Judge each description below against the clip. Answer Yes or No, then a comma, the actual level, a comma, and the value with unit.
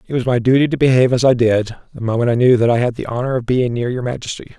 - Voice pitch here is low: Yes, low, 125 Hz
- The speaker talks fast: Yes, fast, 300 wpm